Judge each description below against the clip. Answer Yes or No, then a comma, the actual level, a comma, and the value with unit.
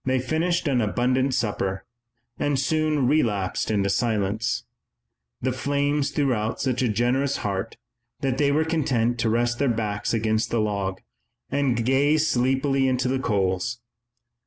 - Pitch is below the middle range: Yes, low, 125 Hz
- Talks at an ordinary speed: Yes, average, 145 wpm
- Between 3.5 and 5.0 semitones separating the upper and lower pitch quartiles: Yes, average, 4.2 semitones